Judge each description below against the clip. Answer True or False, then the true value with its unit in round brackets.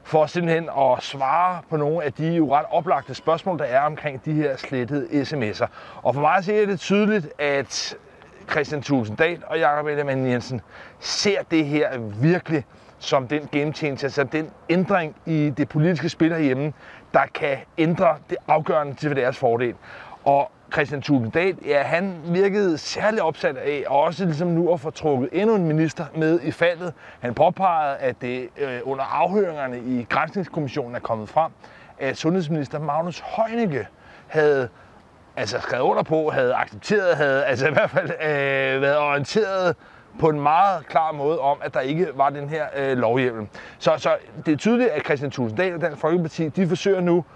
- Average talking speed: True (175 wpm)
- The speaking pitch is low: False (155 Hz)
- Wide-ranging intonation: False (3.5 semitones)